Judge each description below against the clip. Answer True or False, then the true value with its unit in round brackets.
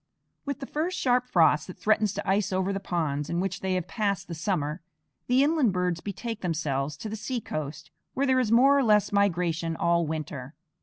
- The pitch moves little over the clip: False (5.5 semitones)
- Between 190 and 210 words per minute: True (200 wpm)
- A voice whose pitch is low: False (190 Hz)